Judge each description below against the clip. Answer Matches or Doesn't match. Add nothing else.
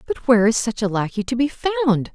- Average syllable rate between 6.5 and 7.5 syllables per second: Matches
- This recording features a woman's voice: Matches